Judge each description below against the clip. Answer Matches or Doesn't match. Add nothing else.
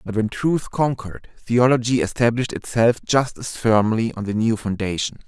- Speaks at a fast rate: Doesn't match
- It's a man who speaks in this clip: Matches